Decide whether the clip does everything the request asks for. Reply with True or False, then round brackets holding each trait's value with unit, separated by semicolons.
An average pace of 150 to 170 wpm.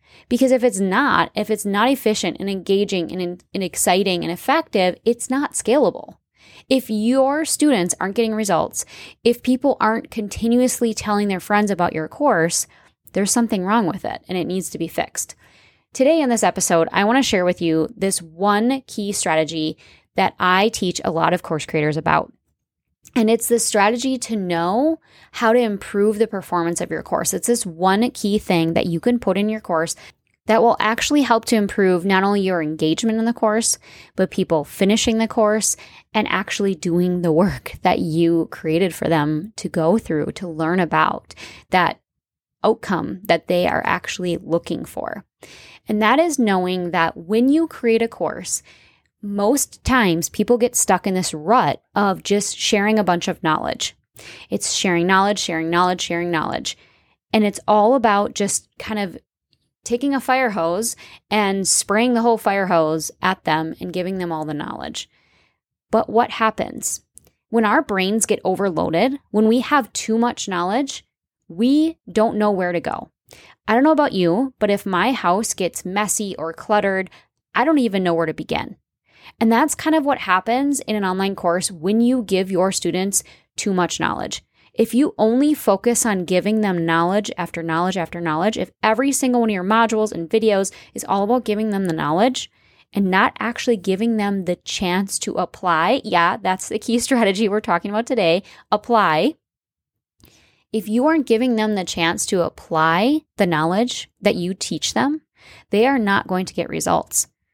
False (180 wpm)